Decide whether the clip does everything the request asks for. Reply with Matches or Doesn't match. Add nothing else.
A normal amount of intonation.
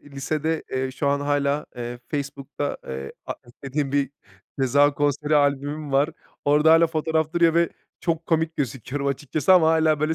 Doesn't match